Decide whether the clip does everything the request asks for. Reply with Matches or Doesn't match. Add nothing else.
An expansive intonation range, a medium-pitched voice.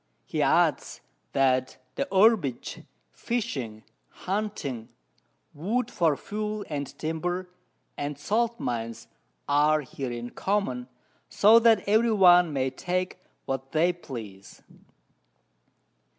Matches